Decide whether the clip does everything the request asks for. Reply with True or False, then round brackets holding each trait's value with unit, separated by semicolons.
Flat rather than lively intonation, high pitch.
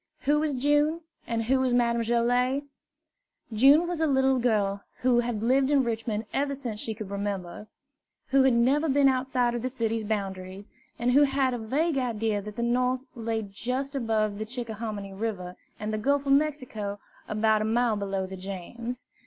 False (3.8 semitones; 235 Hz)